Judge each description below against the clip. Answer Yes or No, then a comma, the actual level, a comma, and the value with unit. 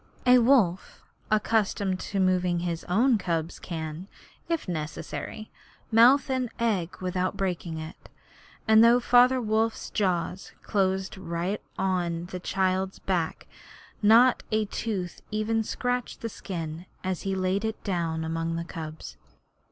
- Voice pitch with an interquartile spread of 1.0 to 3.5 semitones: No, average, 4.3 semitones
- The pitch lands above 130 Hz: Yes, high, 190 Hz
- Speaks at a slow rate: Yes, slow, 130 wpm